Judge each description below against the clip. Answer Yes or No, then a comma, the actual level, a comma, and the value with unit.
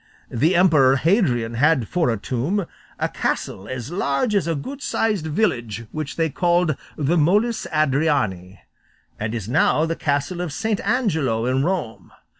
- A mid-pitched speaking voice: Yes, medium, 155 Hz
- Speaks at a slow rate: No, average, 155 wpm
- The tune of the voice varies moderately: No, wide, 6.2 semitones